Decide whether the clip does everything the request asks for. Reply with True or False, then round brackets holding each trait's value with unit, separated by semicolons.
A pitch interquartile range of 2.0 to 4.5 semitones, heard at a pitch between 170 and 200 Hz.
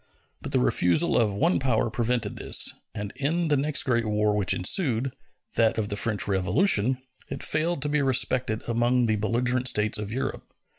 False (4.1 semitones; 120 Hz)